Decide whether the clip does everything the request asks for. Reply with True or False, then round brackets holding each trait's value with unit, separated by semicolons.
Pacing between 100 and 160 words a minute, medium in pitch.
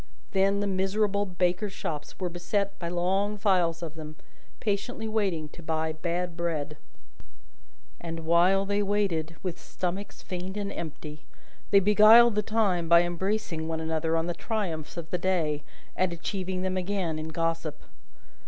True (155 wpm; 180 Hz)